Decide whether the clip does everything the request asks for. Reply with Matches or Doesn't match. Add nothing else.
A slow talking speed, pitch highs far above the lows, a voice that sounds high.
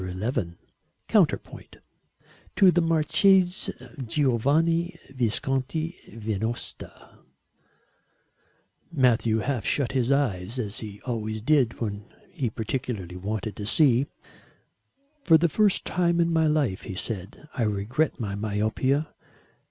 Doesn't match